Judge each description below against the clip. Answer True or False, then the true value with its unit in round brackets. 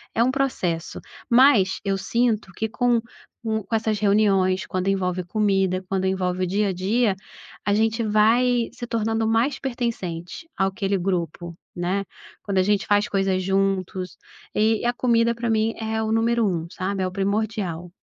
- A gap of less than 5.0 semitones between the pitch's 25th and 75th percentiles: True (3.2 semitones)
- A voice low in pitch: False (205 Hz)